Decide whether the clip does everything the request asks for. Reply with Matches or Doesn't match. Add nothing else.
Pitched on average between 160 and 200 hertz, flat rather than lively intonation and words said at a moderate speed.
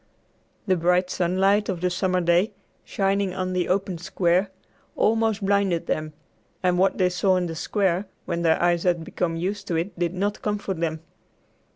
Matches